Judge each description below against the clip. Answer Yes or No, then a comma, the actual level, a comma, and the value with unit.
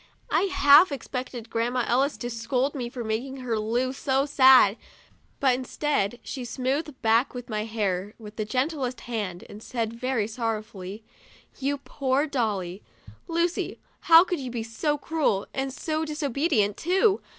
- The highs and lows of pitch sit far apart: No, average, 4.2 semitones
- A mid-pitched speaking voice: No, very high, 255 Hz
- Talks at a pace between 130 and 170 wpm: Yes, average, 150 wpm